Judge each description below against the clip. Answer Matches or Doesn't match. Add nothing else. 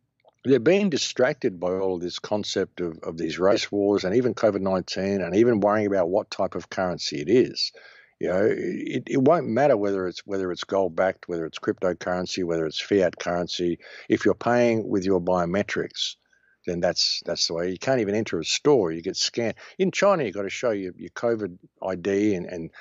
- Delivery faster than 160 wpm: Matches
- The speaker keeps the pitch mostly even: Doesn't match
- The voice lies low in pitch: Matches